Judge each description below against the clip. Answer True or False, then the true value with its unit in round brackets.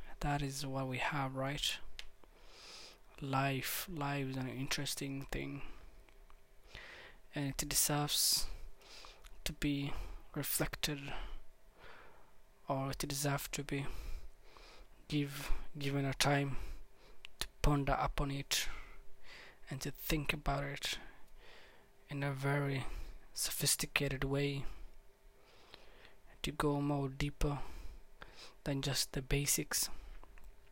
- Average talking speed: False (95 wpm)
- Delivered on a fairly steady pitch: True (1.2 semitones)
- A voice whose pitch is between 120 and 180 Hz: True (140 Hz)